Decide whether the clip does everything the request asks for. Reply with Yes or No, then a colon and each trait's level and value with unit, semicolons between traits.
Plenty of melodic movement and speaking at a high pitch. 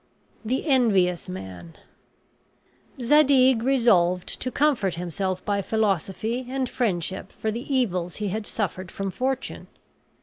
Yes: wide, 5.8 semitones; high, 210 Hz